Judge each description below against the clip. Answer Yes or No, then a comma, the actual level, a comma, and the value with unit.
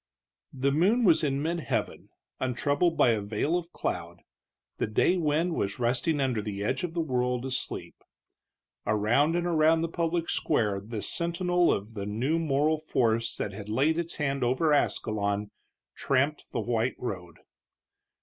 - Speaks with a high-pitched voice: No, low, 135 Hz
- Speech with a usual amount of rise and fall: No, wide, 6.9 semitones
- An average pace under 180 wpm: Yes, average, 160 wpm